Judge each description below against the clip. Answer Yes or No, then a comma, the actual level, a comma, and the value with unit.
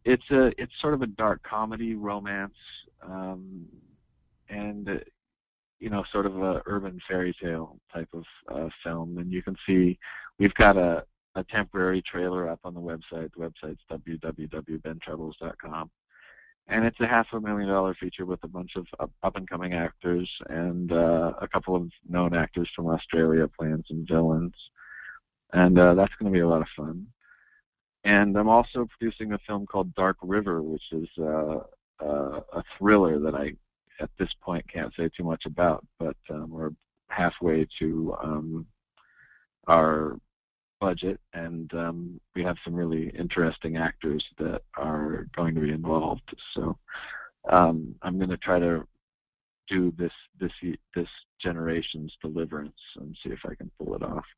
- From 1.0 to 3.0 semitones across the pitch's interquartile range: Yes, average, 2.7 semitones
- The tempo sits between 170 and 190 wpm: No, average, 160 wpm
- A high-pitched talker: No, very low, 85 Hz